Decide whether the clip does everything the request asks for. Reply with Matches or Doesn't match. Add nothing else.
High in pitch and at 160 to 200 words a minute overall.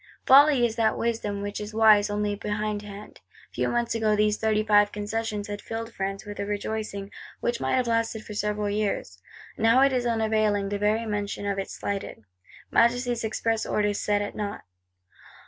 Matches